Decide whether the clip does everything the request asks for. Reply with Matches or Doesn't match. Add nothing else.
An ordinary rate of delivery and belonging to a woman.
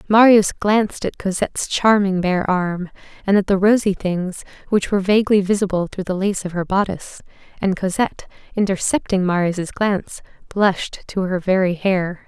Matches